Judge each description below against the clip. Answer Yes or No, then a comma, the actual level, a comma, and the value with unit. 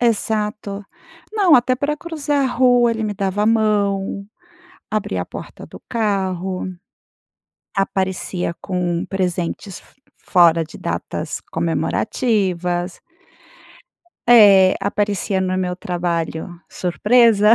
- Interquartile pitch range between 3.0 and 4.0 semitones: Yes, average, 3.6 semitones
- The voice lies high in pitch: Yes, high, 200 Hz